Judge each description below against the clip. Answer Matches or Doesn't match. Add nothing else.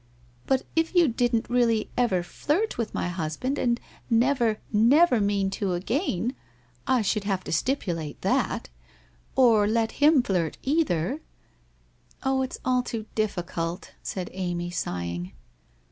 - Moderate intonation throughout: Doesn't match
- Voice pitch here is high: Matches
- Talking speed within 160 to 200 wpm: Doesn't match